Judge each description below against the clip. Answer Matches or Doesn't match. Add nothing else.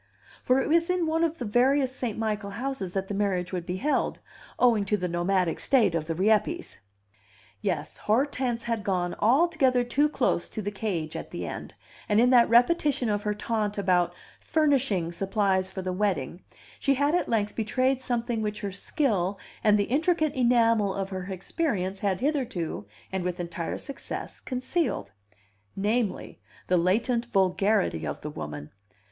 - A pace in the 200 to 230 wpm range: Doesn't match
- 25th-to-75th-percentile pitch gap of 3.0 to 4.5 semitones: Doesn't match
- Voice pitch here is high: Matches